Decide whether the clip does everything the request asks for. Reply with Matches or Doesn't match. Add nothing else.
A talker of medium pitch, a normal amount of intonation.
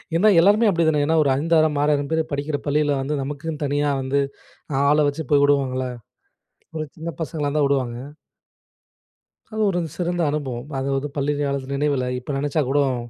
Doesn't match